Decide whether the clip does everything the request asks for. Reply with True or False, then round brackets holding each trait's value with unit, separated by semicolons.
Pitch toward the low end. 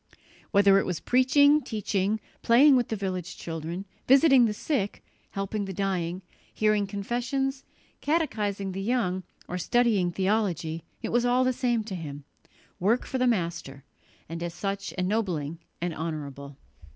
False (200 Hz)